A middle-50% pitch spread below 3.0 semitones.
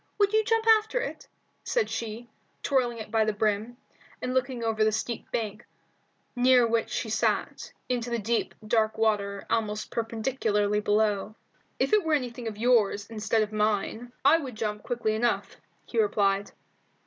Yes: narrow, 2.6 semitones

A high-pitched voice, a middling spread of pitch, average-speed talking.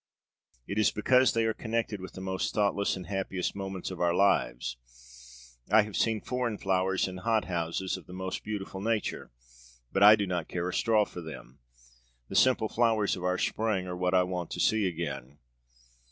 No: very low, 95 Hz; average, 3.3 semitones; average, 185 wpm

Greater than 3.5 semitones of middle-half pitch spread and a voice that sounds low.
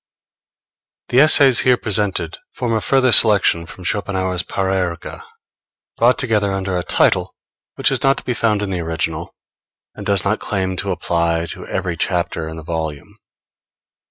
Yes: average, 4.4 semitones; very low, 95 Hz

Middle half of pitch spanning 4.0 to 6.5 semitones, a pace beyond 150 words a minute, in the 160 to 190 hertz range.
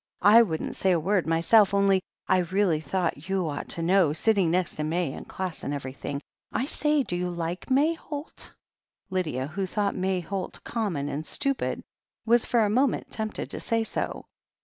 Yes: average, 4.9 semitones; average, 185 wpm; medium, 185 Hz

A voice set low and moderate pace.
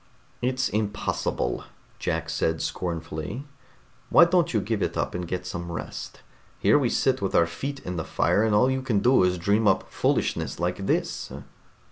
Yes: low, 100 Hz; average, 175 wpm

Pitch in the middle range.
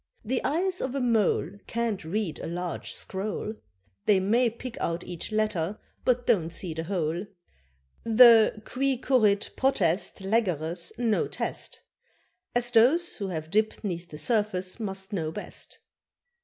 No: high, 210 Hz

